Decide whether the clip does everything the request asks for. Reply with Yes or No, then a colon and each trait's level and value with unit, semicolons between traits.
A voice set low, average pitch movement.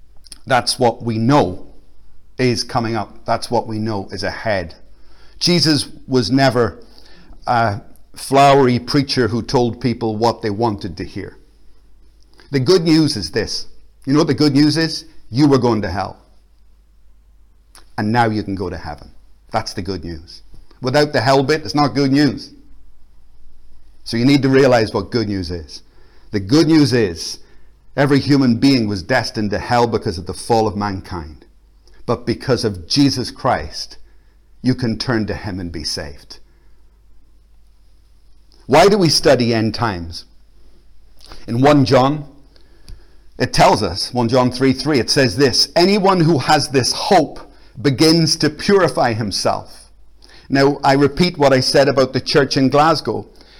No: low, 120 Hz; wide, 5.8 semitones